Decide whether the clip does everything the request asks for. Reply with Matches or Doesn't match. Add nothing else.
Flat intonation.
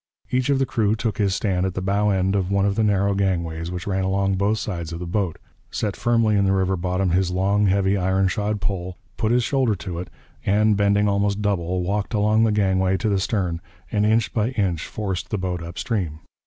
Matches